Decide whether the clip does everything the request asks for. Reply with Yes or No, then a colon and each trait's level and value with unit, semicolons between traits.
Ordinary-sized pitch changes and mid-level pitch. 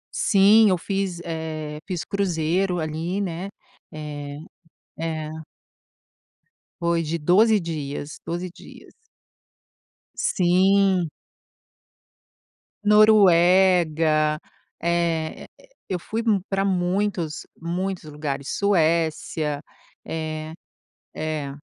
Yes: average, 3.5 semitones; medium, 170 Hz